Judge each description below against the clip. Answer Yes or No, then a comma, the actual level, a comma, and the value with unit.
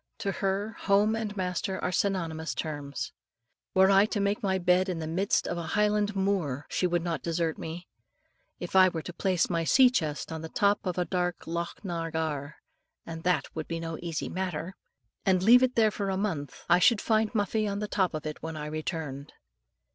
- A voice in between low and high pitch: Yes, medium, 180 Hz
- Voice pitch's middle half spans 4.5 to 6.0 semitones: No, average, 3.6 semitones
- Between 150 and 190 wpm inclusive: No, fast, 205 wpm